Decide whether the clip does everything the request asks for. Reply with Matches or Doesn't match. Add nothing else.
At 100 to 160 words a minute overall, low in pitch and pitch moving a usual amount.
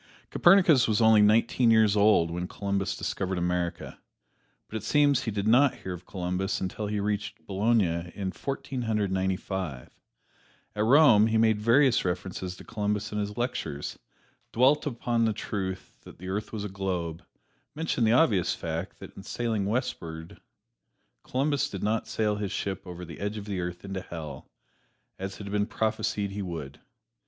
Doesn't match